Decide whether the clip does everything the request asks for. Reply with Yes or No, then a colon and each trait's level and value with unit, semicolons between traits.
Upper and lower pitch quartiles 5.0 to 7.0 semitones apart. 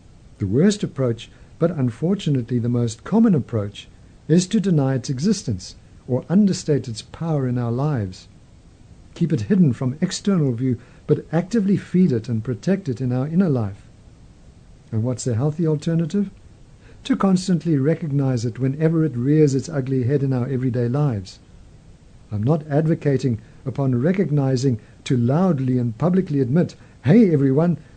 Yes: average, 5.3 semitones